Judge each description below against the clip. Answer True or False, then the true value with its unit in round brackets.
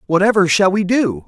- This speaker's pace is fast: False (190 wpm)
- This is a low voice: False (185 Hz)